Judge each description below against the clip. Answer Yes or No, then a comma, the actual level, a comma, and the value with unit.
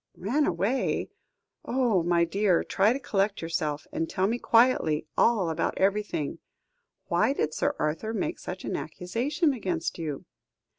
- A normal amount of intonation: No, wide, 6.2 semitones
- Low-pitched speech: No, high, 195 Hz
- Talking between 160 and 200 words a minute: No, average, 145 wpm